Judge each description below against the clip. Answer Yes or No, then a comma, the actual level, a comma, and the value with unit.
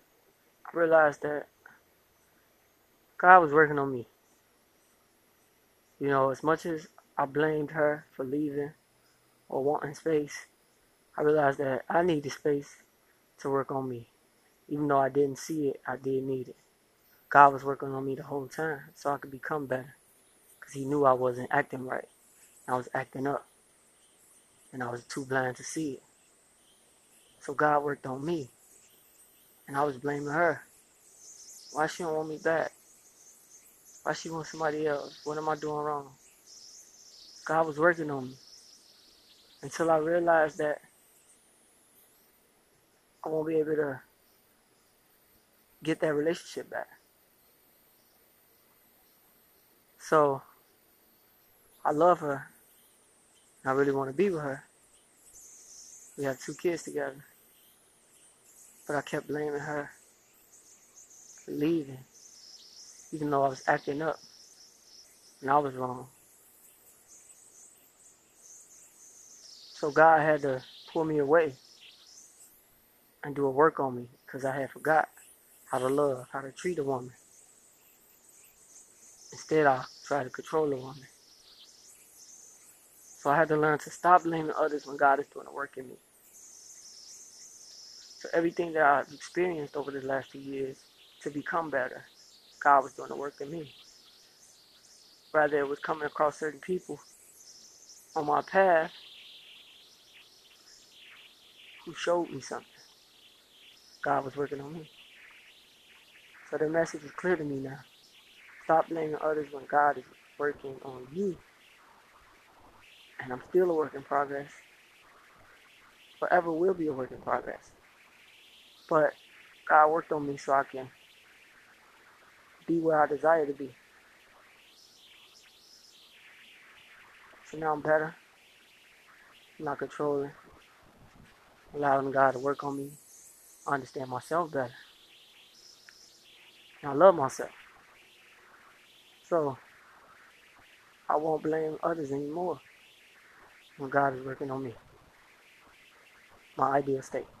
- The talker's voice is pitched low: No, medium, 145 Hz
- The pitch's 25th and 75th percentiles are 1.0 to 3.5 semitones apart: Yes, narrow, 2.5 semitones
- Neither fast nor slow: No, slow, 130 wpm